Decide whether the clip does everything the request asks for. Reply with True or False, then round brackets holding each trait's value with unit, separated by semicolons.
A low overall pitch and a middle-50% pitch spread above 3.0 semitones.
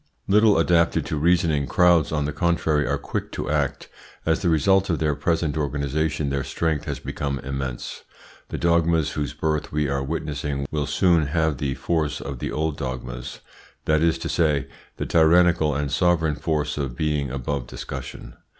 False (75 Hz; 2.7 semitones)